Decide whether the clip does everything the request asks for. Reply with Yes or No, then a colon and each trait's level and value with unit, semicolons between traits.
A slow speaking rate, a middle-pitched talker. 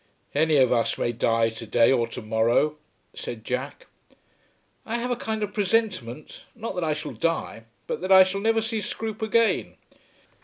No: average, 180 wpm; medium, 160 Hz